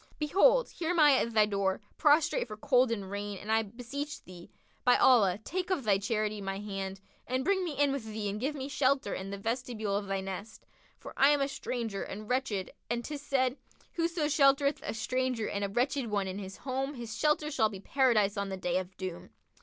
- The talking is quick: Yes, fast, 215 wpm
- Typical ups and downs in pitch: No, wide, 5.7 semitones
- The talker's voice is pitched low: No, high, 230 Hz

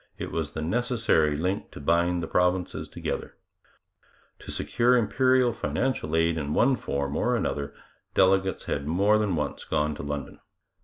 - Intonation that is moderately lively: No, wide, 6.5 semitones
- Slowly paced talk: No, average, 155 wpm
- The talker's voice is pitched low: Yes, very low, 90 Hz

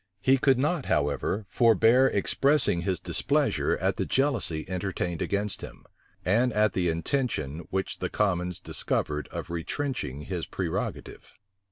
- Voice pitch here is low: Yes, very low, 95 Hz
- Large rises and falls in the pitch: Yes, wide, 6.7 semitones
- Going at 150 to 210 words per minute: No, slow, 135 wpm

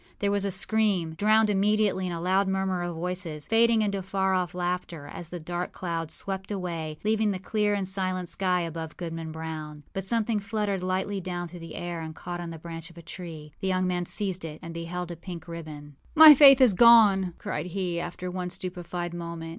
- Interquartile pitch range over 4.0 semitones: No, average, 2.7 semitones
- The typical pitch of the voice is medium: Yes, medium, 180 Hz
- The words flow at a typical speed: No, fast, 210 wpm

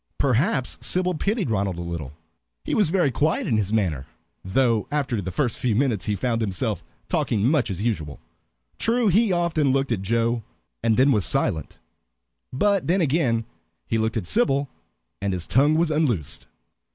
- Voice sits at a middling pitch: No, low, 120 Hz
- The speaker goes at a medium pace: Yes, average, 170 wpm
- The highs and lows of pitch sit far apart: Yes, wide, 7.0 semitones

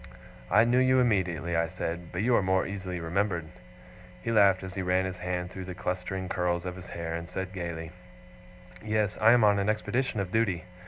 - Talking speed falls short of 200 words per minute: No, fast, 205 wpm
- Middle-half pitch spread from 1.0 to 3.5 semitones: Yes, average, 2.9 semitones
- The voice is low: Yes, very low, 95 Hz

